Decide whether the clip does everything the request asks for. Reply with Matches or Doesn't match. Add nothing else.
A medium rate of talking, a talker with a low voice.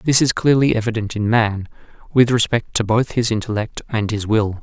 Matches